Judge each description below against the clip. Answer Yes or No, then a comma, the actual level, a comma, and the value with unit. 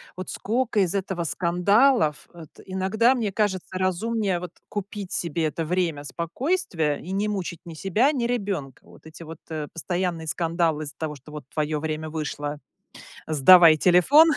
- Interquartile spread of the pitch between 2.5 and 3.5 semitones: No, average, 4.4 semitones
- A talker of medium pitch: Yes, medium, 175 Hz